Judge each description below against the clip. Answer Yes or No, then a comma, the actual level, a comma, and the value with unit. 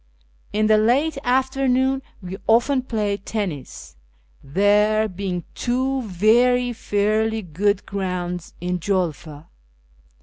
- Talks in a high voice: Yes, high, 210 Hz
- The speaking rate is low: Yes, slow, 100 wpm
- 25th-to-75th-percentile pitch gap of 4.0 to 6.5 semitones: Yes, average, 5.2 semitones